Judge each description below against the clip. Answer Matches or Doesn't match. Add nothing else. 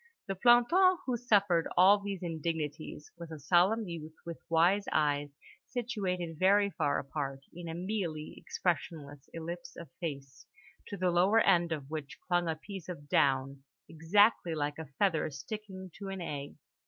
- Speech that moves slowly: Doesn't match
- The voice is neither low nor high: Matches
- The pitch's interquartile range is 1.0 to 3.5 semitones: Doesn't match